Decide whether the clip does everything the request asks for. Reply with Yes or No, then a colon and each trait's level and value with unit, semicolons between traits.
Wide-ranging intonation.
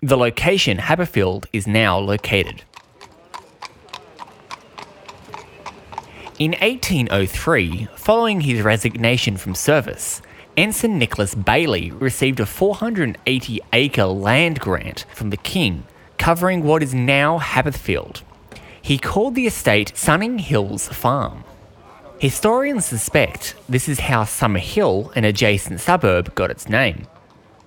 Yes: wide, 7.1 semitones